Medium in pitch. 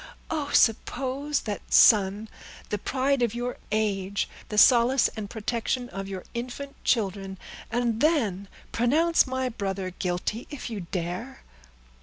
No: high, 230 Hz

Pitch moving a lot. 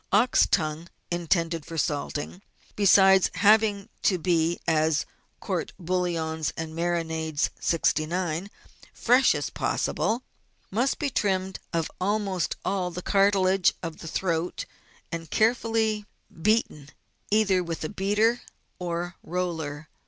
No: average, 3.7 semitones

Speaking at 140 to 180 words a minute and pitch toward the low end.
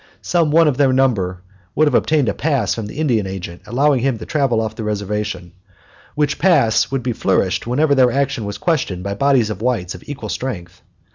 No: fast, 205 wpm; low, 120 Hz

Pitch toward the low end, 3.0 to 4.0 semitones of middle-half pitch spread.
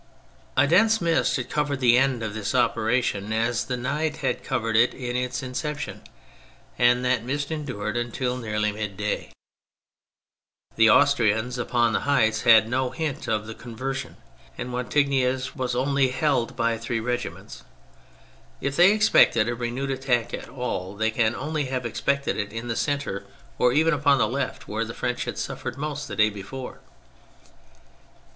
Yes: low, 125 Hz; average, 3.5 semitones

